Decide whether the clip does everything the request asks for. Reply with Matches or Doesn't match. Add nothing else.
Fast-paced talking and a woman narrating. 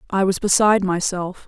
Doesn't match